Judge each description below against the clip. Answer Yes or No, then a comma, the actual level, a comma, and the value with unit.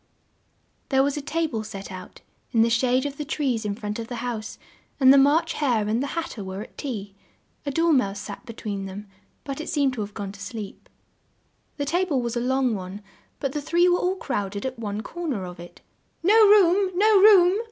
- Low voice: No, very high, 255 Hz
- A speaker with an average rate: No, fast, 230 wpm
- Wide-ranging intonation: Yes, wide, 6.9 semitones